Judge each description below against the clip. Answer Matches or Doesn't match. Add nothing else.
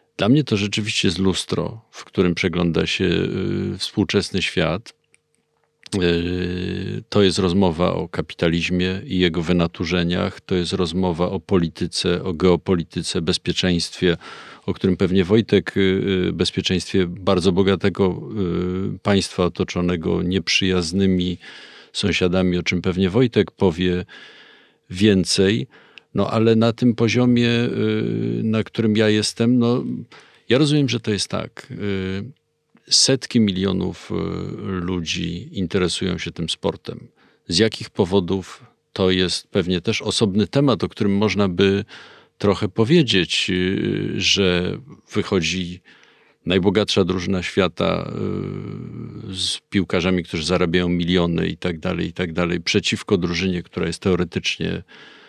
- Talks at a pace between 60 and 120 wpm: Matches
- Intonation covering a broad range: Doesn't match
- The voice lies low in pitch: Matches